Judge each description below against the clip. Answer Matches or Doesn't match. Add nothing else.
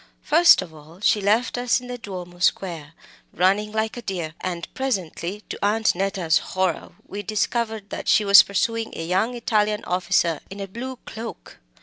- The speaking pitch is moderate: Doesn't match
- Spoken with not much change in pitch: Doesn't match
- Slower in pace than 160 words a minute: Doesn't match